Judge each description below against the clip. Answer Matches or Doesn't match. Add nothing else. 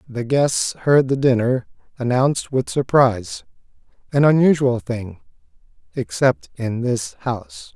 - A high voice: Doesn't match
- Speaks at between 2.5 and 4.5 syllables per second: Matches